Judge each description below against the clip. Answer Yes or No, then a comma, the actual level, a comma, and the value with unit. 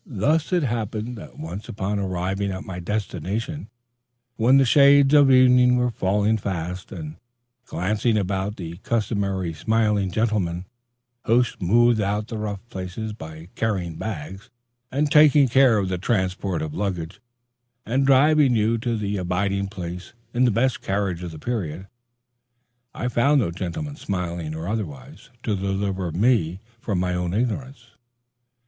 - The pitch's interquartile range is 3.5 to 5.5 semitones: Yes, average, 4.7 semitones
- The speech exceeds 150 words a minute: No, average, 140 wpm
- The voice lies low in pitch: Yes, low, 105 Hz